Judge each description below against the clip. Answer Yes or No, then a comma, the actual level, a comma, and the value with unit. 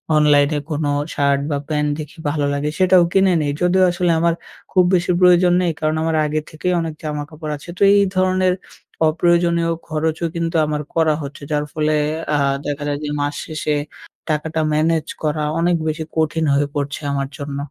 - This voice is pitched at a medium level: Yes, medium, 155 Hz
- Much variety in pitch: No, narrow, 2.5 semitones